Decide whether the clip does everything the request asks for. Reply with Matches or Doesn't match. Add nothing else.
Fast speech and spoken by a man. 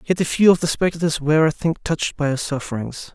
Matches